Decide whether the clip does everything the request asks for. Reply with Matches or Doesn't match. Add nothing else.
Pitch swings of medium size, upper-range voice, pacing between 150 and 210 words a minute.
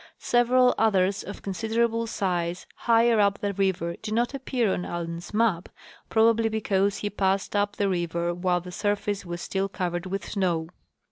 Matches